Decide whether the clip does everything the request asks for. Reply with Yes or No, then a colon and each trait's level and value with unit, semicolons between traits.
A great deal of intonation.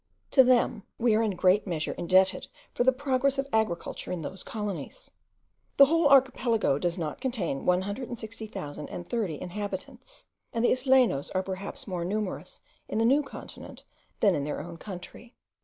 Yes: wide, 5.7 semitones